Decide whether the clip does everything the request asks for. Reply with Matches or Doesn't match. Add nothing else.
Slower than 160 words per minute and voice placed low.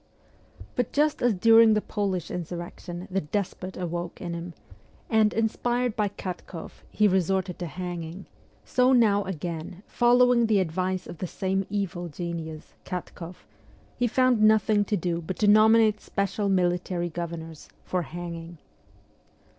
Doesn't match